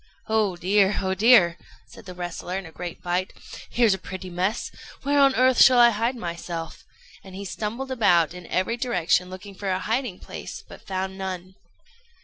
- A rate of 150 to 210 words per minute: Yes, average, 180 wpm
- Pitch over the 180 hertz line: Yes, high, 190 Hz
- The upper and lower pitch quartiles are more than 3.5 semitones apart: Yes, average, 4.2 semitones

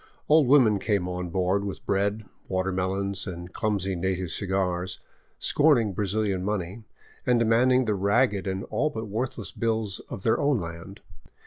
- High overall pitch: No, low, 100 Hz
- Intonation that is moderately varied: Yes, average, 3.3 semitones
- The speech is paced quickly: No, average, 145 wpm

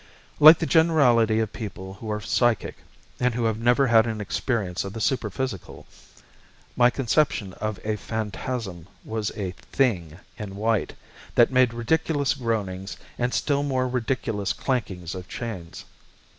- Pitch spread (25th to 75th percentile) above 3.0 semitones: Yes, average, 3.9 semitones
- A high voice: No, low, 115 Hz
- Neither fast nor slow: Yes, average, 145 wpm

